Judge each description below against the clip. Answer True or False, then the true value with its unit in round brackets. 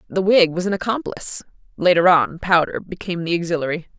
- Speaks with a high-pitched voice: False (180 Hz)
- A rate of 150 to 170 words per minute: True (165 wpm)